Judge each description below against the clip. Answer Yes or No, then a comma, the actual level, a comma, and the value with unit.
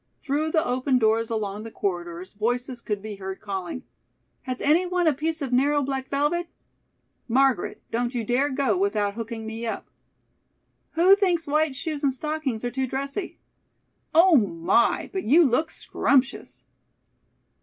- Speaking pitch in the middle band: No, very high, 255 Hz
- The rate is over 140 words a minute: Yes, average, 150 wpm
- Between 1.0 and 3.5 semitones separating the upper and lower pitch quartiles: No, average, 5.3 semitones